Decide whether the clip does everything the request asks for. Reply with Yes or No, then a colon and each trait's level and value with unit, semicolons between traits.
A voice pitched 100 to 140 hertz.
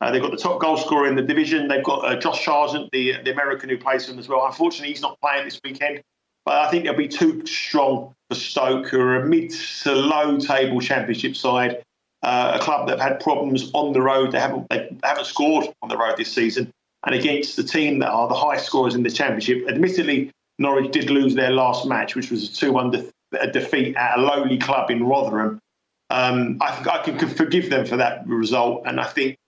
Yes: low, 135 Hz